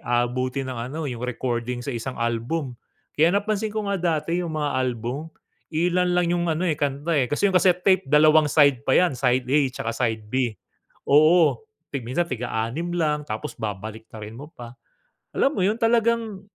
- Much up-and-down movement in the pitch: Yes, wide, 6.1 semitones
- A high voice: No, medium, 145 Hz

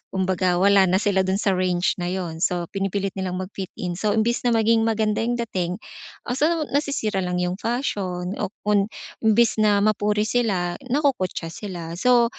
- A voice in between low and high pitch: No, high, 200 Hz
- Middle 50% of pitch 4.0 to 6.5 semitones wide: No, average, 3.6 semitones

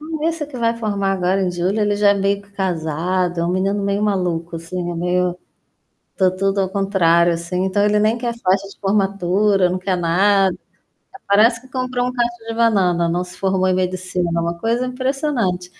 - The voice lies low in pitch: No, high, 195 Hz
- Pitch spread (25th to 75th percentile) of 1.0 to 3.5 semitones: Yes, average, 2.8 semitones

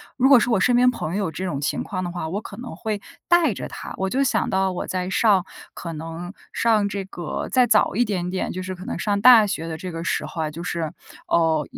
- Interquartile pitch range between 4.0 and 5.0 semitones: Yes, average, 4.5 semitones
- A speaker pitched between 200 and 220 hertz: No, high, 190 Hz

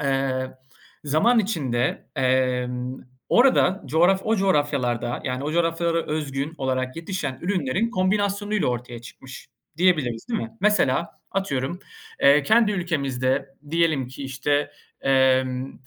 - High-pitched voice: No, medium, 145 Hz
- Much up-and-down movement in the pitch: Yes, wide, 5.9 semitones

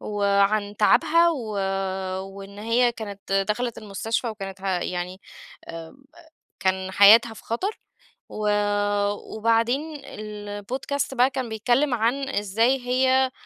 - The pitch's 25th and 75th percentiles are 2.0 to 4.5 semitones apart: Yes, average, 4.0 semitones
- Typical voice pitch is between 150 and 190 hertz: No, high, 220 Hz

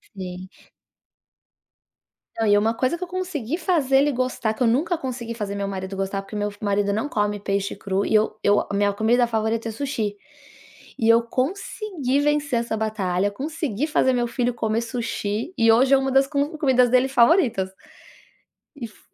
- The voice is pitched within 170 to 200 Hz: No, high, 230 Hz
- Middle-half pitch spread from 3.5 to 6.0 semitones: Yes, average, 4.7 semitones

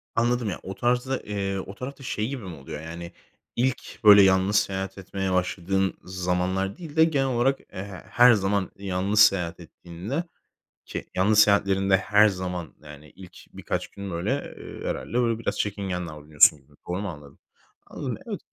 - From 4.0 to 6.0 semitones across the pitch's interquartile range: No, average, 3.3 semitones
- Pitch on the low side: Yes, very low, 95 Hz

